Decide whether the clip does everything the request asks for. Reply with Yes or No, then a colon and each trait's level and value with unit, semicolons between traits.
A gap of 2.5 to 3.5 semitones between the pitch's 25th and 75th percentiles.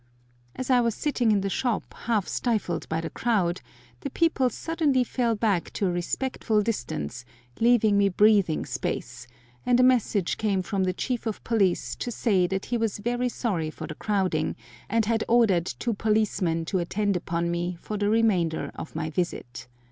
No: average, 4.9 semitones